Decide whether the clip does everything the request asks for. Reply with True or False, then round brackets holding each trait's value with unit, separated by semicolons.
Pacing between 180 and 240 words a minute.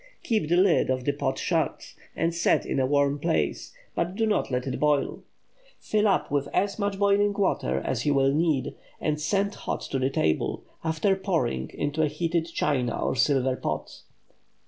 True (185 wpm)